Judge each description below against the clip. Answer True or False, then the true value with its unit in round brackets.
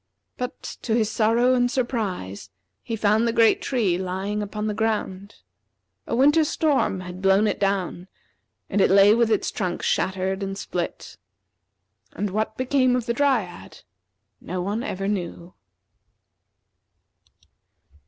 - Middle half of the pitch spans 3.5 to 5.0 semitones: True (3.8 semitones)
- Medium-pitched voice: False (210 Hz)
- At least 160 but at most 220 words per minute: False (135 wpm)